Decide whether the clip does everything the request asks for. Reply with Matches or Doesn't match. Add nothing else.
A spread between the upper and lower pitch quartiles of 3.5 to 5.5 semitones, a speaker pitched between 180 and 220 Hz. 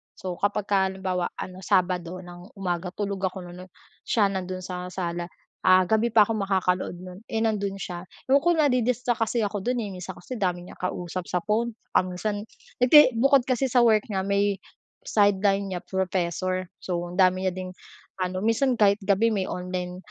Doesn't match